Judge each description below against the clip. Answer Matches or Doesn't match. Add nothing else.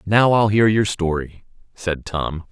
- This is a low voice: Matches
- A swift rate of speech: Doesn't match